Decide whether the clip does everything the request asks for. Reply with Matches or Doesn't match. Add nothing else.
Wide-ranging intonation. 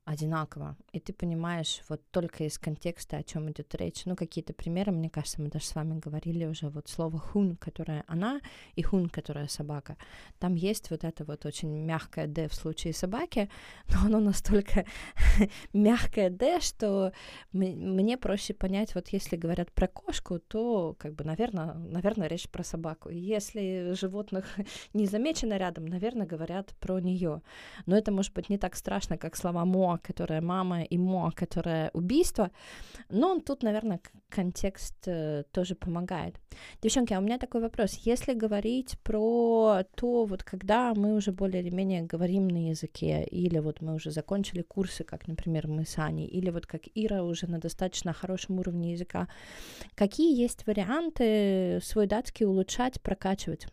Doesn't match